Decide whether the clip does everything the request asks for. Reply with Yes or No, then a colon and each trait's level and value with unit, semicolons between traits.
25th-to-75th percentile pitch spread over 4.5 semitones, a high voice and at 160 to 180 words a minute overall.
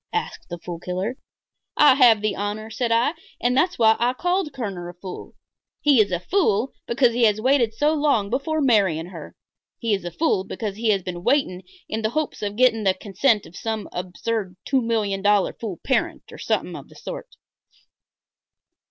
No: average, 4.9 semitones; high, 220 Hz; average, 190 wpm